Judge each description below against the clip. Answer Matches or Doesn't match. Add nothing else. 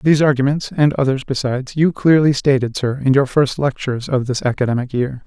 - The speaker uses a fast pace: Doesn't match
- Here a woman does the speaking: Doesn't match